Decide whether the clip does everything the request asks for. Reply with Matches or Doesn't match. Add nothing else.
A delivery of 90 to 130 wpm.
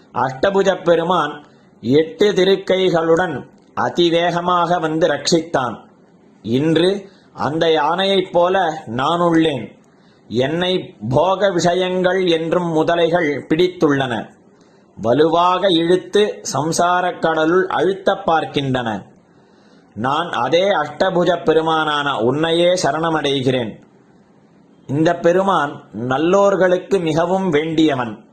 Doesn't match